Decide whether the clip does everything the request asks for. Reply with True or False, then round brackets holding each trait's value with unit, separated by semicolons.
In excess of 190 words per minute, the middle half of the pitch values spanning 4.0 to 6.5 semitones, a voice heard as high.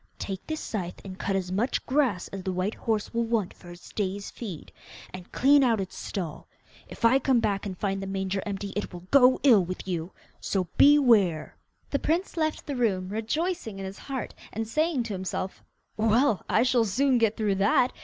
True (200 wpm; 4.8 semitones; 210 Hz)